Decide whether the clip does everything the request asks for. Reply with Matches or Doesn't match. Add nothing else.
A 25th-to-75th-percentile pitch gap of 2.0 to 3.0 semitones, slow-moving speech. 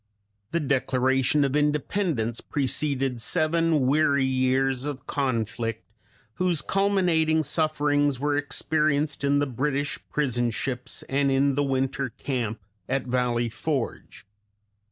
Matches